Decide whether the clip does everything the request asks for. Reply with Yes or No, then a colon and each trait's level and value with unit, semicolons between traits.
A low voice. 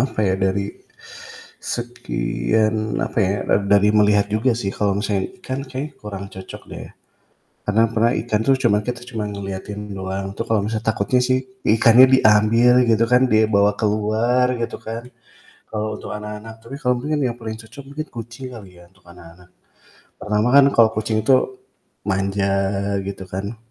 Yes: low, 110 Hz